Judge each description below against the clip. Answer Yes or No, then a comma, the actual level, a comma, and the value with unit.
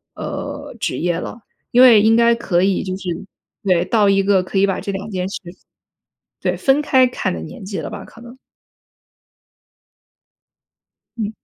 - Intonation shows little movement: No, average, 4.0 semitones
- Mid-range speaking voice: No, high, 200 Hz